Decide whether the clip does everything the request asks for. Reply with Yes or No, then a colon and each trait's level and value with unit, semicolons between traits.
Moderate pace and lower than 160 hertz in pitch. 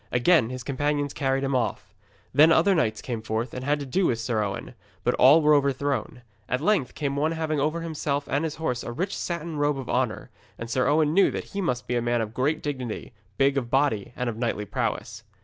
No: fast, 225 wpm; medium, 140 Hz